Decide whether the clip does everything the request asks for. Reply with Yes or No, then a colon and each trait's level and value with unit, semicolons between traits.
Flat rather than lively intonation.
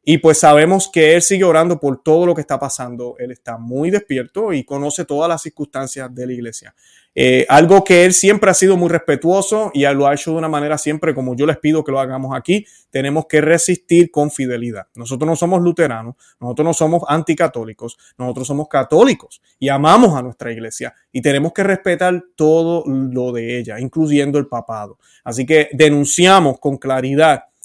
No: average, 4.5 semitones